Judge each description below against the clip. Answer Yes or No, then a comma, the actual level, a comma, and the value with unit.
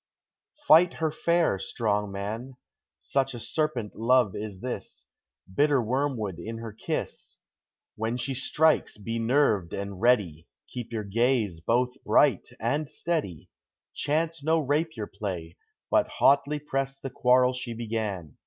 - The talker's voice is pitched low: Yes, low, 120 Hz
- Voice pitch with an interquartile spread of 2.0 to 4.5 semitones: No, average, 5.2 semitones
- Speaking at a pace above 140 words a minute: No, slow, 135 wpm